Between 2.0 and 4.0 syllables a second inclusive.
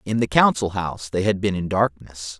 No: 5.3 syllables/s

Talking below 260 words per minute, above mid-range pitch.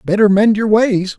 Yes: fast, 205 wpm; high, 210 Hz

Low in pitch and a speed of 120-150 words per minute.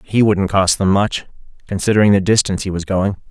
No: low, 100 Hz; average, 200 wpm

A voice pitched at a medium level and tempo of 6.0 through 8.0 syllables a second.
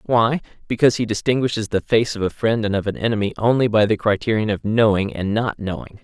No: low, 110 Hz; 6.1 syllables/s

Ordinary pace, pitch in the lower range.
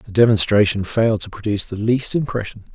Yes: average, 175 wpm; low, 110 Hz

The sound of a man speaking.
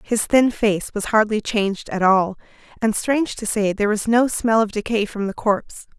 No: female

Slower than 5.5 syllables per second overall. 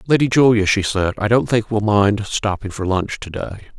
Yes: 5.1 syllables/s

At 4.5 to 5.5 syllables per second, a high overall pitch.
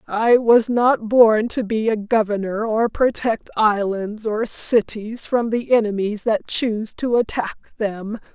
No: 3.9 syllables/s; high, 220 Hz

